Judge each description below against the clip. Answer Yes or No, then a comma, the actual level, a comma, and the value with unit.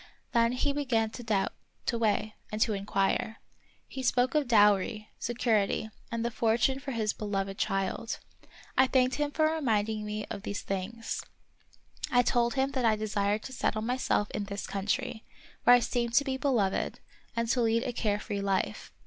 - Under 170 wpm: No, average, 175 wpm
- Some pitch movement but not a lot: Yes, average, 3.2 semitones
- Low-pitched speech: No, high, 225 Hz